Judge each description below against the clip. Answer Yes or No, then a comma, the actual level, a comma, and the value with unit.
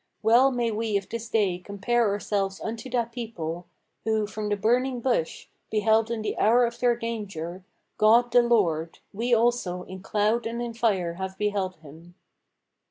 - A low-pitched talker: No, high, 220 Hz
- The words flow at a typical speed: Yes, average, 165 wpm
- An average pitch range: Yes, average, 3.5 semitones